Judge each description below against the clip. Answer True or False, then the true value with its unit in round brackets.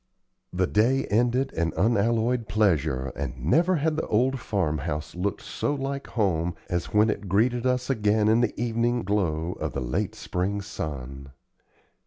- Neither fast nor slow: True (160 wpm)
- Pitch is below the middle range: True (105 Hz)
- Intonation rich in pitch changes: True (6.4 semitones)